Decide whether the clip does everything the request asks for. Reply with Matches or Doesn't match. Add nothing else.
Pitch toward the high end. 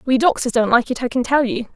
Matches